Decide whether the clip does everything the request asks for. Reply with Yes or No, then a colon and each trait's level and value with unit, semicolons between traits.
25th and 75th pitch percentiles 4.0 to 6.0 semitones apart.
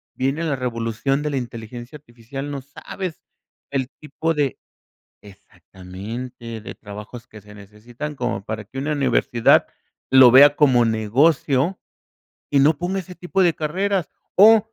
Yes: average, 4.8 semitones